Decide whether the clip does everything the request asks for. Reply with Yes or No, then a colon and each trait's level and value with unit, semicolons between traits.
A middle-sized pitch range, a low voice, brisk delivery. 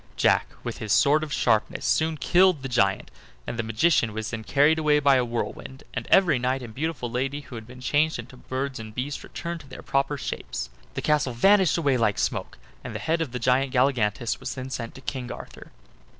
Yes: average, 3.7 semitones; low, 130 Hz; fast, 215 wpm